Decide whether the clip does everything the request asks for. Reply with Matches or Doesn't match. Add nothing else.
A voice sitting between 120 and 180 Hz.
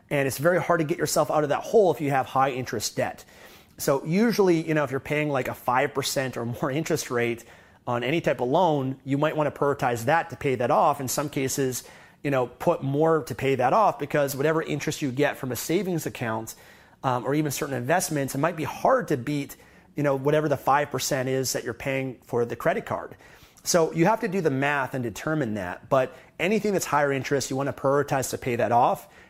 Matches